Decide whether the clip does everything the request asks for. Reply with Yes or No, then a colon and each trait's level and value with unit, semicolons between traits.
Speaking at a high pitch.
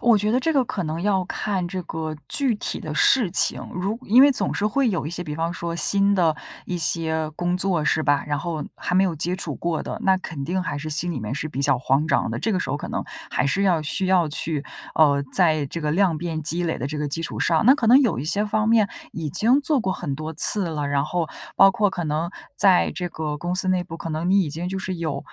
No: medium, 170 Hz